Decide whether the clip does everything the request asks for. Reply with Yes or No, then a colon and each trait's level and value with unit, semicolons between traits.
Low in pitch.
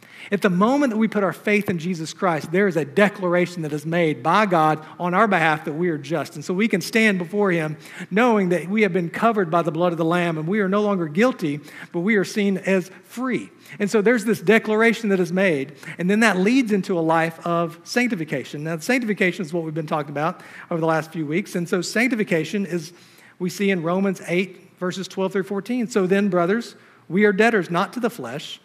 No: medium, 185 Hz